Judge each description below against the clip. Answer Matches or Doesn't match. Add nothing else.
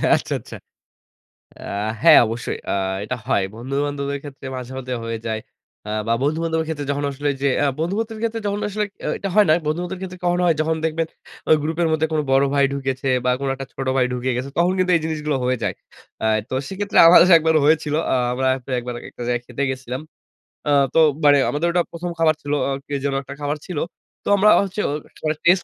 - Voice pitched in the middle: Matches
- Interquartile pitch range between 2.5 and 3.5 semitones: Doesn't match